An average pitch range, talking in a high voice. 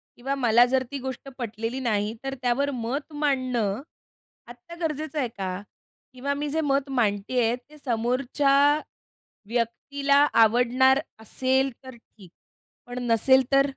Yes: average, 3.0 semitones; very high, 260 Hz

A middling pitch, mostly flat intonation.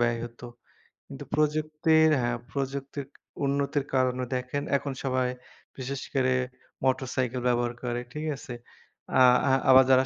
No: low, 130 Hz; narrow, 1.9 semitones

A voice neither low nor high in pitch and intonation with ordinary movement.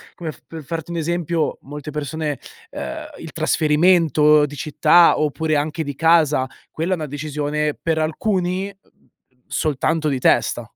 No: medium, 155 Hz; narrow, 2.0 semitones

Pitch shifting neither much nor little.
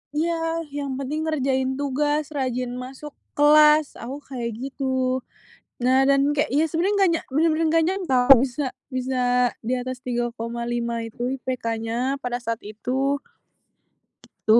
Yes: average, 3.2 semitones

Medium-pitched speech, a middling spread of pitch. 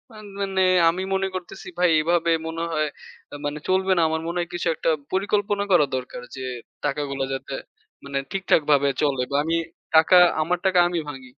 Yes: medium, 165 Hz; average, 4.3 semitones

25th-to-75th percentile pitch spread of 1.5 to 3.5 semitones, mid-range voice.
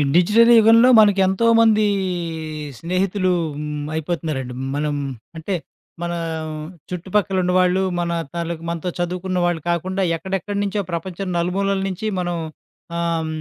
Yes: narrow, 2.6 semitones; medium, 180 Hz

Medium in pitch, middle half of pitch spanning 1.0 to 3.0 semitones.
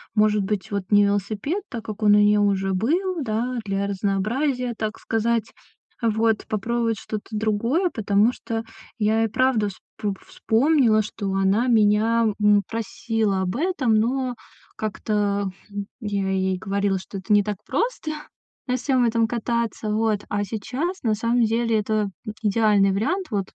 No: high, 215 Hz; narrow, 2.4 semitones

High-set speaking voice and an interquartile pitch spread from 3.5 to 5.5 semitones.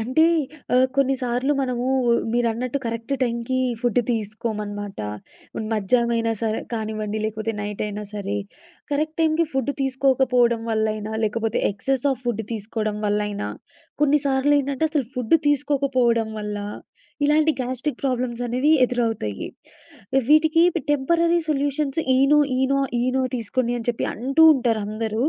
Yes: high, 245 Hz; average, 3.8 semitones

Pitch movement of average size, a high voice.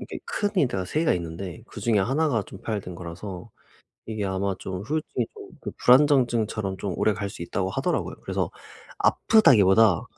No: average, 4.4 semitones; low, 105 Hz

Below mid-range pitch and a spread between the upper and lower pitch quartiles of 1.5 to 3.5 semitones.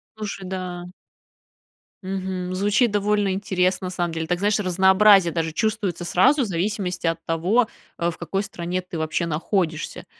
No: medium, 185 Hz; average, 2.8 semitones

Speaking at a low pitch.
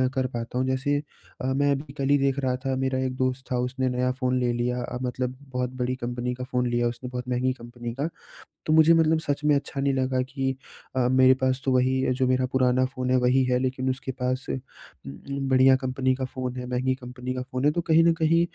Yes: low, 130 Hz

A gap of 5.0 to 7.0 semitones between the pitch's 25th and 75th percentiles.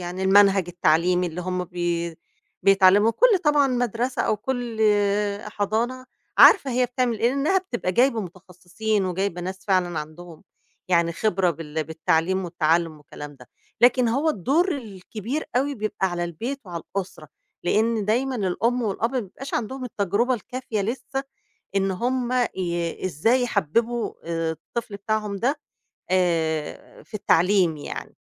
Yes: wide, 5.5 semitones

